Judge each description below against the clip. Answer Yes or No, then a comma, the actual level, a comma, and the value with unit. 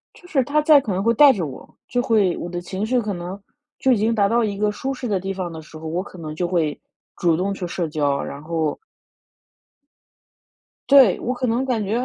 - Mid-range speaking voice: No, high, 195 Hz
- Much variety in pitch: Yes, wide, 5.7 semitones